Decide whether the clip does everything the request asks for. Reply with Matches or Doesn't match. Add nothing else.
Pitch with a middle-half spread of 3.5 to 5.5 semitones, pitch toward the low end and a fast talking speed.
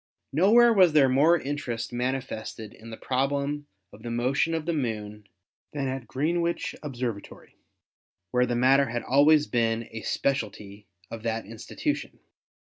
Doesn't match